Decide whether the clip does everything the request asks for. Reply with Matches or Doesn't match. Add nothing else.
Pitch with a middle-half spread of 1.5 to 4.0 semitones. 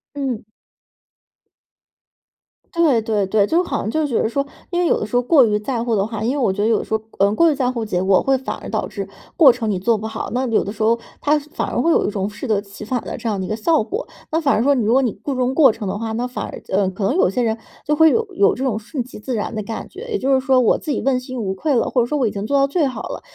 Doesn't match